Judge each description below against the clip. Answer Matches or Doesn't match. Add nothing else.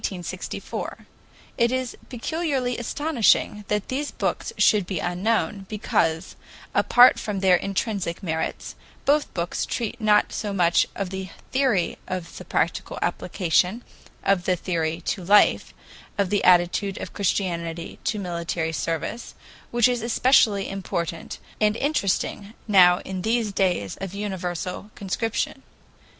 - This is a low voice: Doesn't match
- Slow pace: Matches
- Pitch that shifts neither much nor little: Matches